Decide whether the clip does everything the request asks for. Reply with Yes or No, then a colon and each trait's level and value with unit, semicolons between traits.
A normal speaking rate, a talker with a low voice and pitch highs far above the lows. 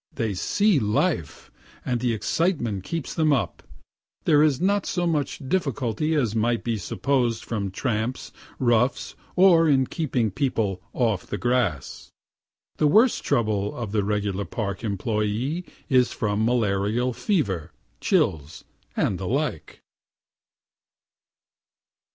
No: slow, 120 wpm; low, 120 Hz; wide, 6.0 semitones